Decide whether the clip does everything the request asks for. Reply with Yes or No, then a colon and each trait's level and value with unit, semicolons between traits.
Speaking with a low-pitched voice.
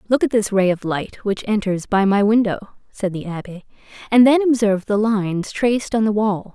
No: high, 210 Hz